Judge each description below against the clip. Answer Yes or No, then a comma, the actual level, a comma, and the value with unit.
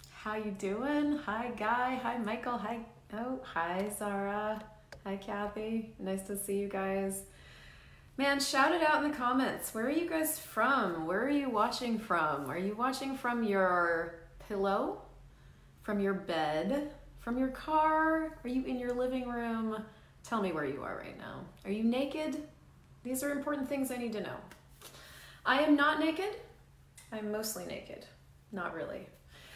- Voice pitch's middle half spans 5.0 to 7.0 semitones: Yes, average, 5.3 semitones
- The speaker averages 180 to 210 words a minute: No, average, 160 wpm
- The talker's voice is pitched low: No, high, 235 Hz